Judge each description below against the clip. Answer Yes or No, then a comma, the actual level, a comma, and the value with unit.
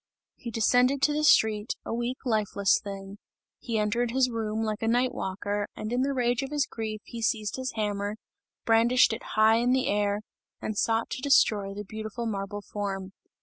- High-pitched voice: Yes, high, 220 Hz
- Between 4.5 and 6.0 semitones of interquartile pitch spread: No, average, 2.9 semitones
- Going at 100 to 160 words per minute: No, average, 190 wpm